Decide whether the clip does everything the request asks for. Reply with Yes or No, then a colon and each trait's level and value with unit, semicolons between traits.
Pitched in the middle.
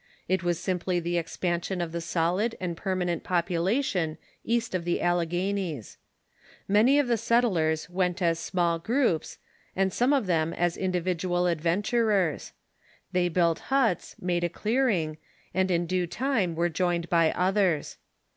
Yes: medium, 180 Hz